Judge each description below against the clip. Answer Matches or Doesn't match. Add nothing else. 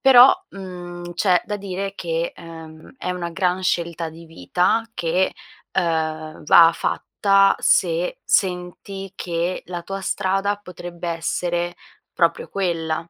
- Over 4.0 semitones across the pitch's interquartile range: Doesn't match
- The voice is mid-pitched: Matches